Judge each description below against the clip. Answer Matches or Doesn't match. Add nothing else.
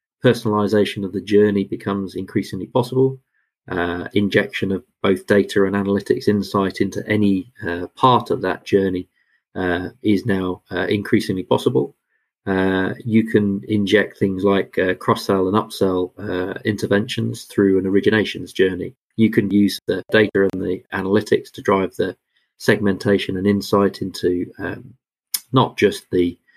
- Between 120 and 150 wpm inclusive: Matches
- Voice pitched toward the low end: Matches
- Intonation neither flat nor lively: Doesn't match